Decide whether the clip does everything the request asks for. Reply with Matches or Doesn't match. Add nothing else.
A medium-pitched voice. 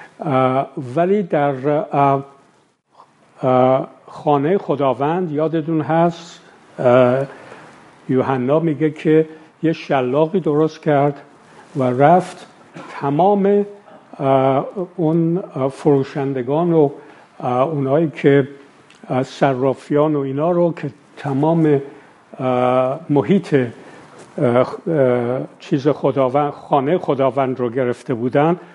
Matches